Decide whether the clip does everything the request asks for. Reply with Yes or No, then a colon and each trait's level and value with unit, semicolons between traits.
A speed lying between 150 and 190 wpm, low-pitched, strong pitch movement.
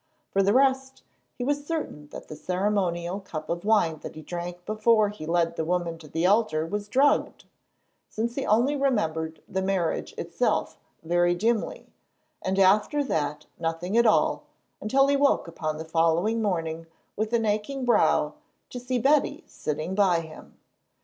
No: average, 165 wpm; high, 195 Hz; wide, 6.0 semitones